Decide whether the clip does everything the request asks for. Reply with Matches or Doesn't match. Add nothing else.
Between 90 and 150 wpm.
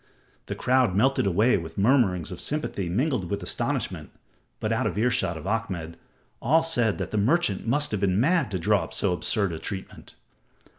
Doesn't match